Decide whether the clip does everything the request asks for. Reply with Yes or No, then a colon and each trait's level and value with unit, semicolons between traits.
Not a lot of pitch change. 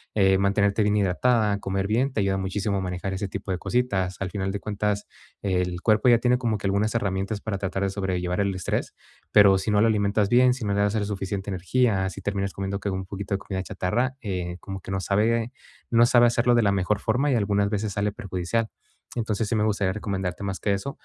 Yes: narrow, 2.2 semitones